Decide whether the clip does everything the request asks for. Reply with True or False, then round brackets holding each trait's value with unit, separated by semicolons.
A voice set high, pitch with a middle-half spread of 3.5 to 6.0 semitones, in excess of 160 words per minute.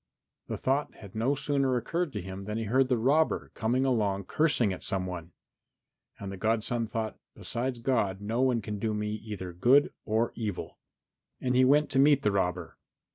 False (115 Hz; 4.5 semitones; 185 wpm)